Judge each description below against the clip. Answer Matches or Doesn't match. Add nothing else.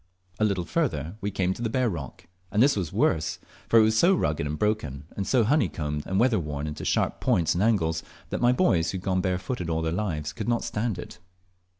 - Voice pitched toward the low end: Matches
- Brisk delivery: Matches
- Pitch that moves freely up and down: Matches